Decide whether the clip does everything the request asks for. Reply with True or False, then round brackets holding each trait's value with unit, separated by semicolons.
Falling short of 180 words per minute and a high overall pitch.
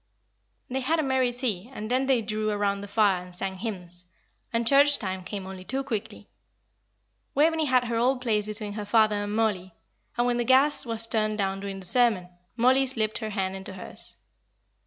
False (195 wpm; 220 Hz)